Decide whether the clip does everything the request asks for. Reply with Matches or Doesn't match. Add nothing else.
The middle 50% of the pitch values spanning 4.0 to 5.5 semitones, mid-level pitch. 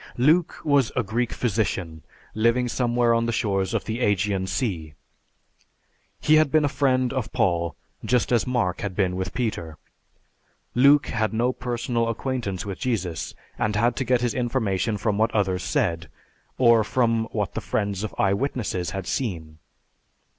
Doesn't match